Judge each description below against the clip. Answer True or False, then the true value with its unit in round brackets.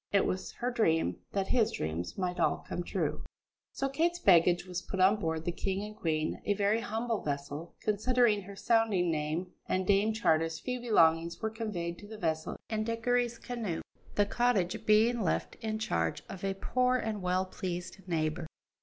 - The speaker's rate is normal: True (180 wpm)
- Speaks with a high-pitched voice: True (195 Hz)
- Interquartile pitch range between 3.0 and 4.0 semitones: False (4.8 semitones)